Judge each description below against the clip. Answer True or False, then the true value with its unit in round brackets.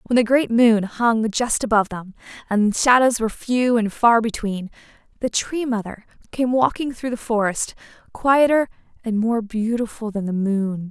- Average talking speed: True (165 wpm)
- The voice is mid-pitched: False (225 Hz)